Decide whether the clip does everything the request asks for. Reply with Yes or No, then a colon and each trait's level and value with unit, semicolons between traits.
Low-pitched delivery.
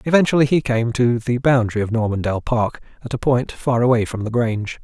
Yes: low, 120 Hz